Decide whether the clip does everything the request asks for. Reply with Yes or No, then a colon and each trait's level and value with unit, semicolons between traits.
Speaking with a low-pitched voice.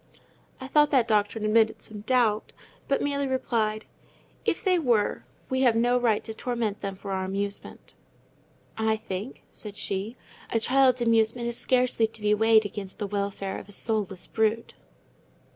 No: high, 220 Hz